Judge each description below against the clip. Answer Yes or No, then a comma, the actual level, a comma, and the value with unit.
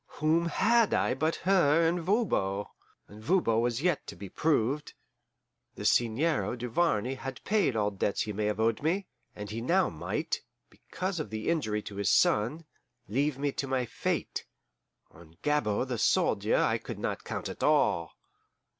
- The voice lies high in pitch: No, low, 130 Hz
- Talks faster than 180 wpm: No, average, 165 wpm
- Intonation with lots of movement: Yes, wide, 7.5 semitones